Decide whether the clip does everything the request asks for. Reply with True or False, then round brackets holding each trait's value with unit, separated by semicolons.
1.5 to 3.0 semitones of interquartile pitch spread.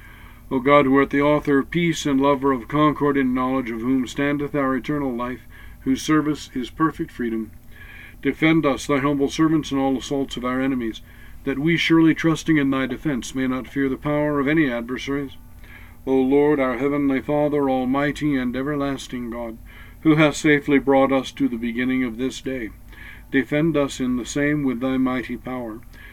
True (2.6 semitones)